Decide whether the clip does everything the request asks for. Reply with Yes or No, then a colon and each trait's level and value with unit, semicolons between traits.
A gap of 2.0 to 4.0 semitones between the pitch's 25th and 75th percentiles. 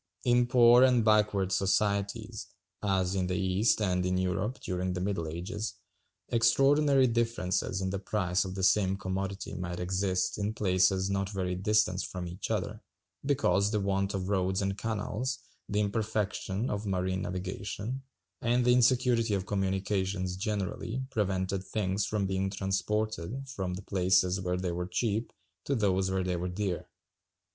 Yes: narrow, 2.6 semitones